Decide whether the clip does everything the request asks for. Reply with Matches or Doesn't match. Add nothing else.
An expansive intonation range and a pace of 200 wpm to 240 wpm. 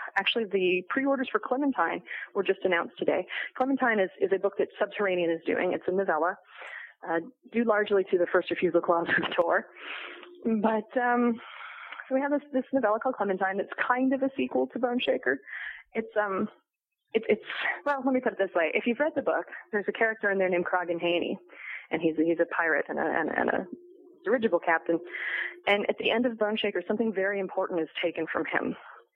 Matches